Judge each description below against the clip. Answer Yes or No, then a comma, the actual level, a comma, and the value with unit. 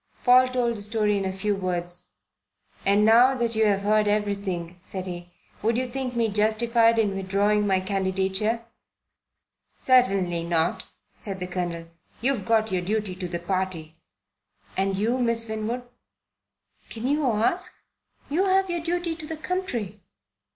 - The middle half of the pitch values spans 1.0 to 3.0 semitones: No, average, 4.0 semitones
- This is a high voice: Yes, high, 210 Hz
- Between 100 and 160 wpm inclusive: Yes, average, 150 wpm